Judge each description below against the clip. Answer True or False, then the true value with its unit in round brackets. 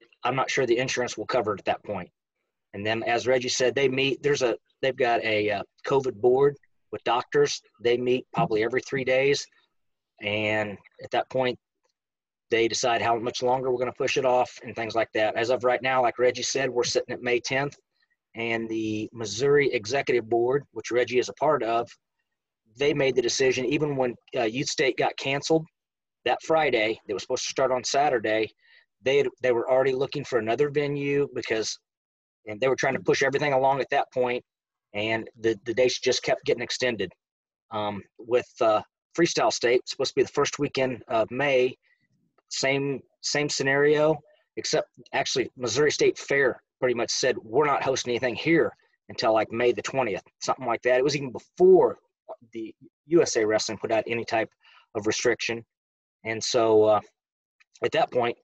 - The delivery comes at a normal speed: True (185 wpm)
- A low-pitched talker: True (130 Hz)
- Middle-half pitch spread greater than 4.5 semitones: False (4.1 semitones)